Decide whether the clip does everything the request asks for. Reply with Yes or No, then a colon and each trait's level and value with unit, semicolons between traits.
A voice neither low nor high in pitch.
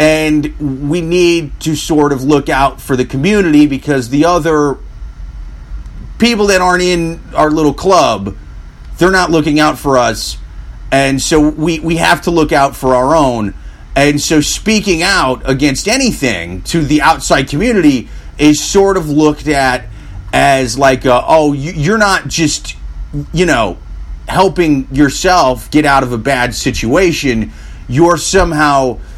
Yes: medium, 145 Hz